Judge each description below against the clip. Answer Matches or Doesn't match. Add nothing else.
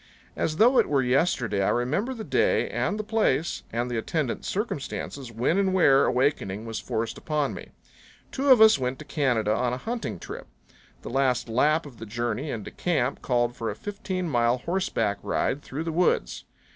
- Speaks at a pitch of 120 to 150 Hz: Matches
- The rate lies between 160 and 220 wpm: Matches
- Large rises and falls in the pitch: Matches